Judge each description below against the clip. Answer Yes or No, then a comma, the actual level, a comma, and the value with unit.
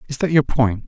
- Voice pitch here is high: No, low, 130 Hz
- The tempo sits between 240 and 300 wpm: Yes, fast, 275 wpm